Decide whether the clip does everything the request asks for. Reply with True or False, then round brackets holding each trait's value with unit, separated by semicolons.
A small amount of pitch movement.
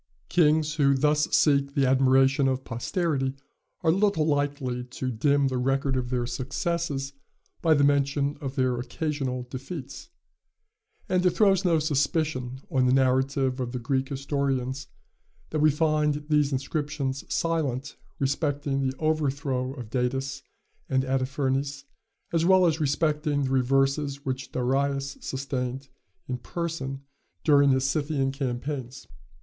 True (2.3 semitones)